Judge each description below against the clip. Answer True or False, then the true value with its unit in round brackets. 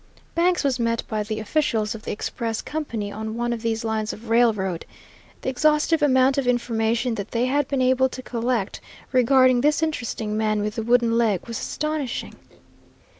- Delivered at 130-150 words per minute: False (175 wpm)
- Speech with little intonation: False (3.0 semitones)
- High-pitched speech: True (235 Hz)